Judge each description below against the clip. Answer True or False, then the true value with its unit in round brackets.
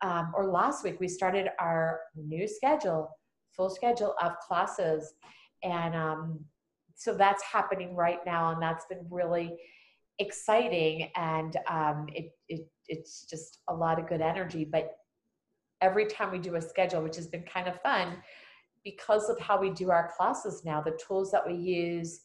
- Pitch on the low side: False (175 Hz)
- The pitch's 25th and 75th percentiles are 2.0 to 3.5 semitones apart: True (2.9 semitones)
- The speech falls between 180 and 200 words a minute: False (165 wpm)